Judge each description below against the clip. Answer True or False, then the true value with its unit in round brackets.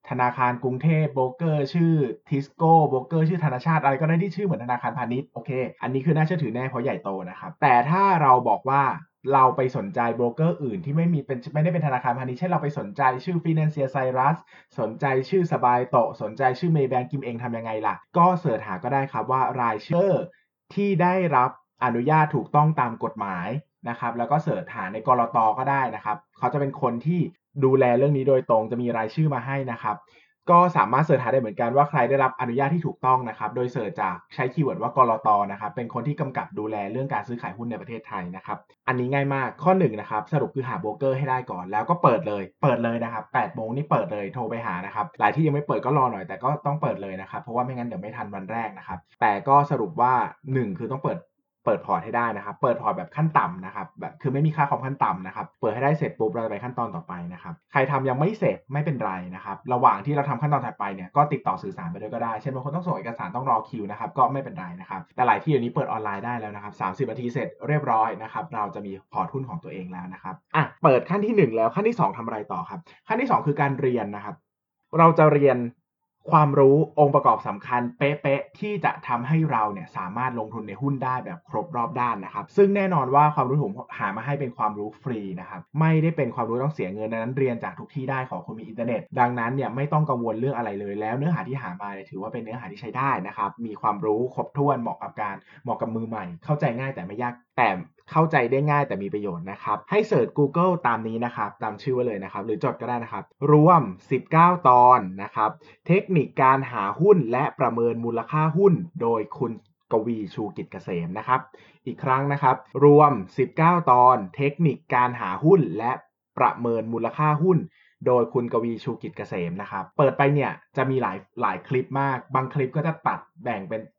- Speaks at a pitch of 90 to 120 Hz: False (135 Hz)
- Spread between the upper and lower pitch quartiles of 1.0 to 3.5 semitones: False (4.2 semitones)